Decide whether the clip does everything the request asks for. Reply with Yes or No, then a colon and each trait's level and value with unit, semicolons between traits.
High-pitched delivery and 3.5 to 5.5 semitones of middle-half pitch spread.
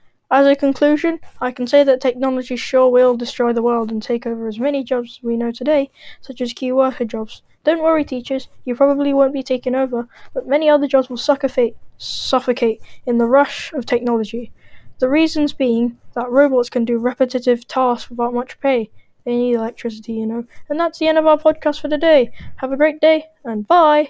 No: very high, 255 Hz; average, 3.1 semitones